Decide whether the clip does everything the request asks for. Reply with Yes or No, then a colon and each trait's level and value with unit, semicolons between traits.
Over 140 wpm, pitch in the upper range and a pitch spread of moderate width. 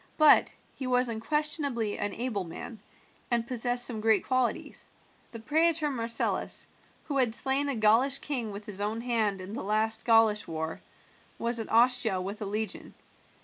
Yes: average, 160 wpm; high, 230 Hz; average, 3.2 semitones